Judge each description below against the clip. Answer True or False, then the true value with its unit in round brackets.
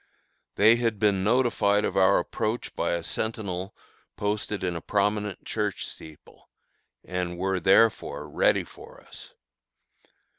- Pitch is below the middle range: True (100 Hz)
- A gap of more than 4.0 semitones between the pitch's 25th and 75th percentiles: False (2.8 semitones)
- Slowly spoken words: True (125 wpm)